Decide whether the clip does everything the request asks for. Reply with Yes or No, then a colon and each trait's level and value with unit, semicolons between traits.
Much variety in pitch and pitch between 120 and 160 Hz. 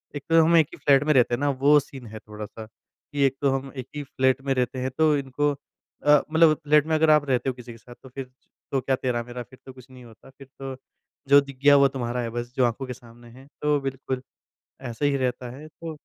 No: narrow, 2.5 semitones; low, 135 Hz